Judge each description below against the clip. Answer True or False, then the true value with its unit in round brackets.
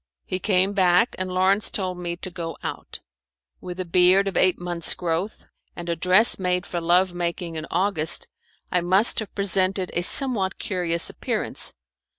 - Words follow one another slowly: False (165 wpm)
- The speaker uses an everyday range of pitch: False (1.6 semitones)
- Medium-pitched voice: True (180 Hz)